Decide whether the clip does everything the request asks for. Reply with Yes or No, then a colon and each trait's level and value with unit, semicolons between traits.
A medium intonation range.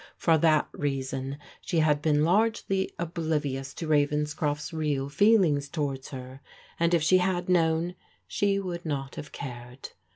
Yes: average, 3.4 semitones